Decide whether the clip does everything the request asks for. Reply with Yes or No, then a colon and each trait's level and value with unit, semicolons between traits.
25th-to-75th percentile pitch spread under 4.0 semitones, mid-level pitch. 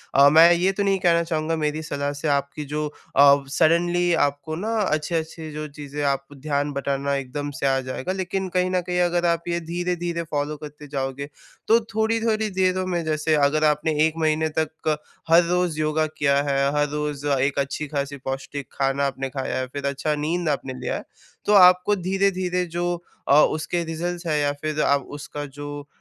Yes: average, 3.6 semitones; medium, 155 Hz